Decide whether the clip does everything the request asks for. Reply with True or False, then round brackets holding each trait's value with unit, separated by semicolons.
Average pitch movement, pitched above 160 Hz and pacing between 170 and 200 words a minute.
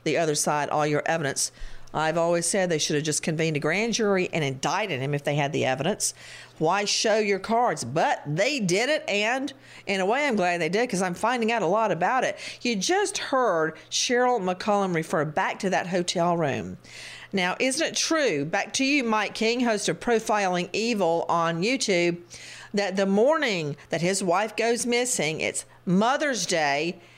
False (5.8 semitones; 185 Hz; 190 wpm)